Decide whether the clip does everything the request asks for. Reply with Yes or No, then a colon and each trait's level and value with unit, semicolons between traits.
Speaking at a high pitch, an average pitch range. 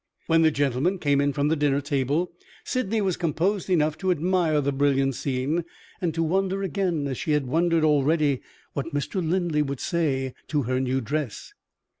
No: medium, 150 Hz; average, 3.7 semitones